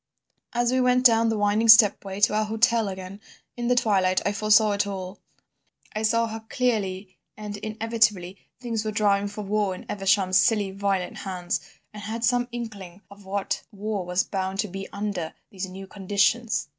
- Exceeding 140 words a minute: Yes, average, 180 wpm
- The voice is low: No, high, 205 Hz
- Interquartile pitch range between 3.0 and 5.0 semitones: No, narrow, 2.5 semitones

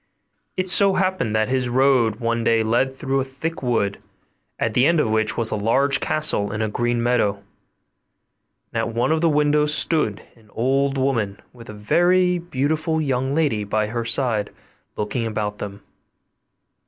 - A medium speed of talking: Yes, average, 170 wpm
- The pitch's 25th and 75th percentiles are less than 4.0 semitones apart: No, average, 5.2 semitones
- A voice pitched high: No, low, 125 Hz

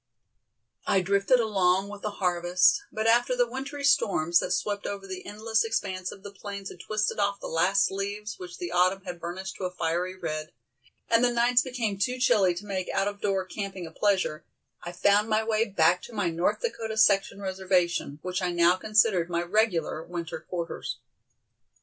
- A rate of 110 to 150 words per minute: No, average, 185 wpm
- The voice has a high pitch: Yes, high, 195 Hz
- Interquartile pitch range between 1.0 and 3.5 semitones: Yes, average, 3.1 semitones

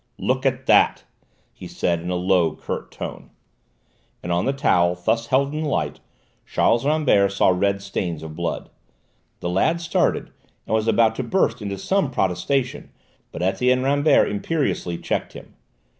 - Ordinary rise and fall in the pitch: No, wide, 7.1 semitones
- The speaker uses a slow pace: No, average, 160 wpm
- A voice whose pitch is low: Yes, low, 110 Hz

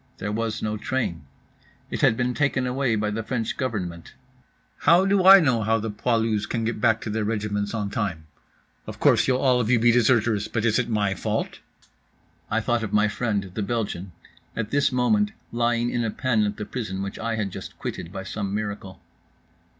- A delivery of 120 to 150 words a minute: No, average, 200 wpm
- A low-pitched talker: Yes, low, 110 Hz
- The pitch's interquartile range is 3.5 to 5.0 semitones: No, average, 2.9 semitones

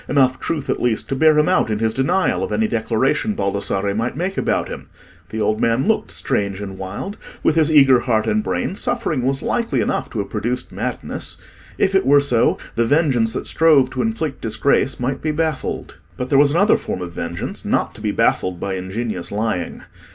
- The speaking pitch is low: Yes, low, 130 Hz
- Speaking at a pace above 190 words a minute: Yes, fast, 205 wpm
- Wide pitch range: Yes, wide, 6.3 semitones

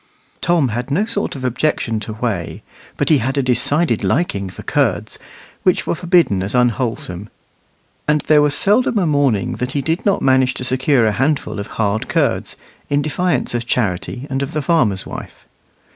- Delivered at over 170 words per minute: Yes, average, 180 wpm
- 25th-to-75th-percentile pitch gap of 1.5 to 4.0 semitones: No, average, 5.3 semitones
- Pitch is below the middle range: Yes, low, 130 Hz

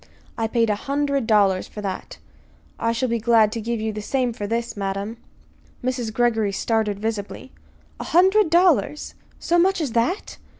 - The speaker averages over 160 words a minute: Yes, average, 170 wpm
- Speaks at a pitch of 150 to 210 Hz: No, high, 230 Hz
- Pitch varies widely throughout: No, average, 4.2 semitones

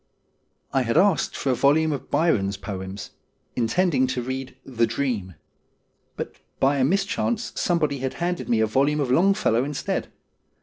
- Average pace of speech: Yes, average, 160 wpm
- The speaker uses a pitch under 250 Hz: Yes, low, 135 Hz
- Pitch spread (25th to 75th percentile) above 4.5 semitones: Yes, average, 5.3 semitones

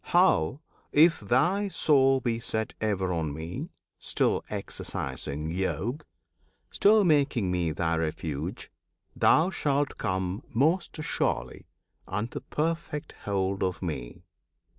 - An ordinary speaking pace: No, slow, 110 wpm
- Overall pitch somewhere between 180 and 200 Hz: No, low, 105 Hz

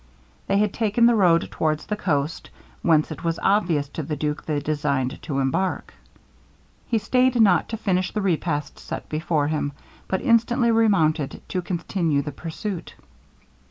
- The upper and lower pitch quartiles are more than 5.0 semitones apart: Yes, wide, 5.6 semitones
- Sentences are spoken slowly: No, average, 160 wpm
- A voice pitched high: No, medium, 170 Hz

